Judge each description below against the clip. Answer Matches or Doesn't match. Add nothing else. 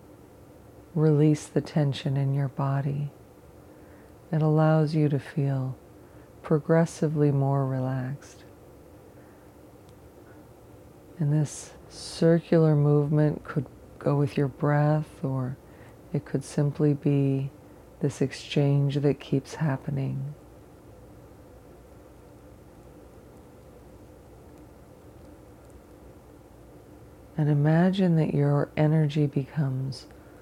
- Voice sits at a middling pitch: Matches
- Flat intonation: Matches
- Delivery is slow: Matches